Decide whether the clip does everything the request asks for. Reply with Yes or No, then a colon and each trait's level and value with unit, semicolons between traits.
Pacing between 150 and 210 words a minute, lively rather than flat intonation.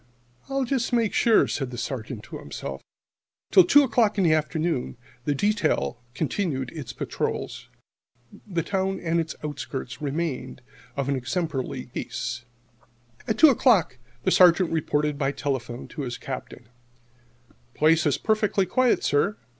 No: average, 140 wpm; wide, 6.6 semitones